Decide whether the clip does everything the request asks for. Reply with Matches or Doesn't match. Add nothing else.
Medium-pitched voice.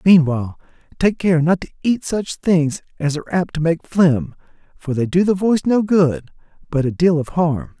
Matches